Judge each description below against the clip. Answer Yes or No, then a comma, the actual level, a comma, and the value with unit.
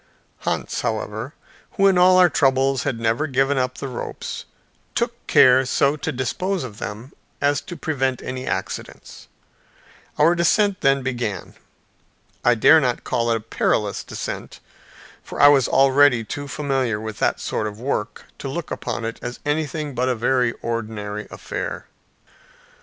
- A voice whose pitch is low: Yes, low, 130 Hz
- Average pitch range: Yes, average, 3.8 semitones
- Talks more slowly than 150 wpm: No, average, 155 wpm